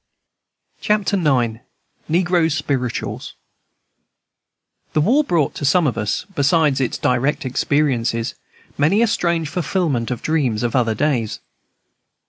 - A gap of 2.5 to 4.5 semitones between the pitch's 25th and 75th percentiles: No, wide, 5.5 semitones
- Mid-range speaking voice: Yes, medium, 145 Hz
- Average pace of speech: No, slow, 115 wpm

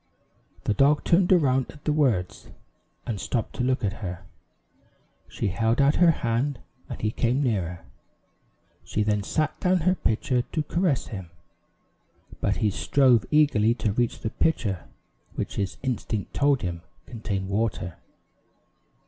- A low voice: Yes, low, 120 Hz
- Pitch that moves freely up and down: Yes, wide, 5.7 semitones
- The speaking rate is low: No, average, 145 wpm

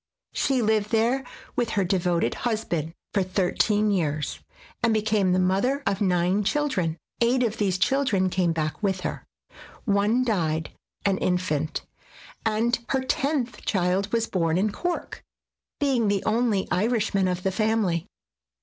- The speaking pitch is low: No, high, 200 Hz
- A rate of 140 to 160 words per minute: Yes, average, 145 wpm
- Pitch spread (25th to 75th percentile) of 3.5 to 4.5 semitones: Yes, average, 4.0 semitones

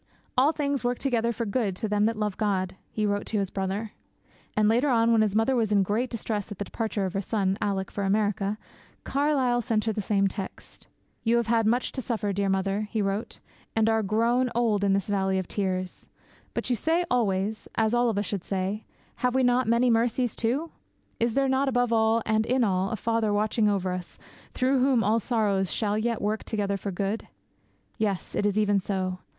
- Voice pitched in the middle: No, high, 215 Hz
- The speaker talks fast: Yes, fast, 210 wpm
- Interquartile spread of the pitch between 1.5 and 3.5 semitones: Yes, average, 2.9 semitones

